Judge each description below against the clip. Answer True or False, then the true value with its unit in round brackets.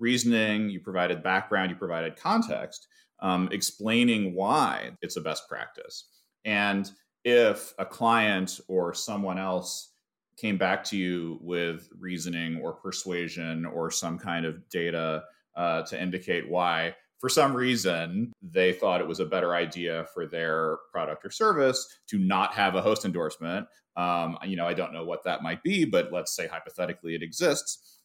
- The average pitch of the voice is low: True (95 Hz)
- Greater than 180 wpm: False (160 wpm)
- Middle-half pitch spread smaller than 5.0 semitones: False (5.3 semitones)